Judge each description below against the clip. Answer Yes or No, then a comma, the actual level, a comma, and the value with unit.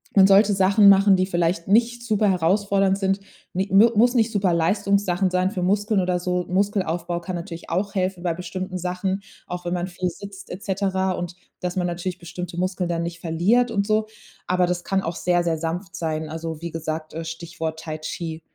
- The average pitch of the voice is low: No, medium, 185 Hz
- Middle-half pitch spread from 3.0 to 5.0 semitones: No, narrow, 2.5 semitones